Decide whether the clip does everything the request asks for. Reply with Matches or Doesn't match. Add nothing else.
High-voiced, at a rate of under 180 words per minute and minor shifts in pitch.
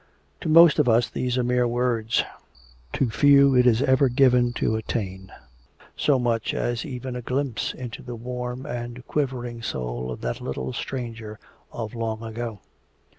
Doesn't match